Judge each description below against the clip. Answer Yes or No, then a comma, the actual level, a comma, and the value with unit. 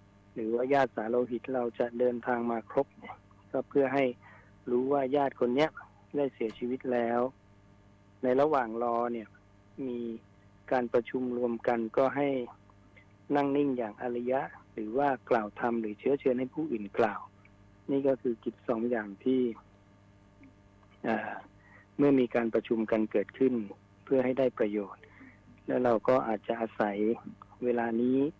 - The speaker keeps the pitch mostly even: No, average, 4.3 semitones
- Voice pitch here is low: Yes, low, 120 Hz